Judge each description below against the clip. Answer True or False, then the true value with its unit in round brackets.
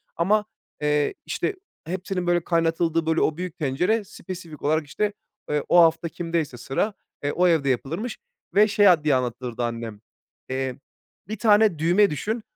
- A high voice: False (165 Hz)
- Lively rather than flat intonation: False (4.6 semitones)